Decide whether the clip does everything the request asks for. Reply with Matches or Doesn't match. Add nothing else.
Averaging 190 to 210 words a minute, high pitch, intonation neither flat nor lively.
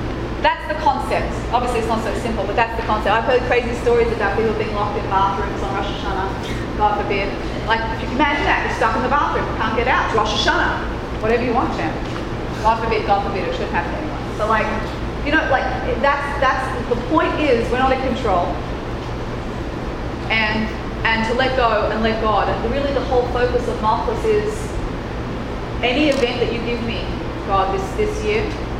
Matches